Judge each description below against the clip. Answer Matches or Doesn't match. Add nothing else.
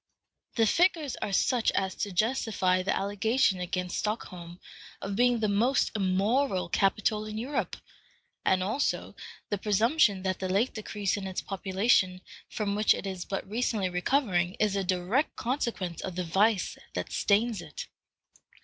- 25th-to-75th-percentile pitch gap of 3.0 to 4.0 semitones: Matches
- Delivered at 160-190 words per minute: Doesn't match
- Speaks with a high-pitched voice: Matches